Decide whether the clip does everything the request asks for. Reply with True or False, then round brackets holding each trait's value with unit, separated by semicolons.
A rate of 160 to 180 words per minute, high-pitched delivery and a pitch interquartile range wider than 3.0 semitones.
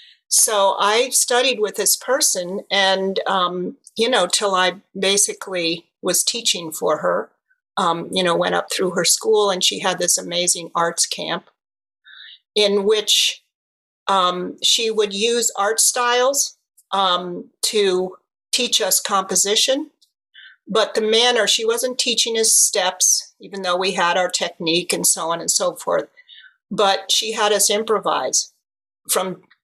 False (145 wpm; 200 Hz; 3.9 semitones)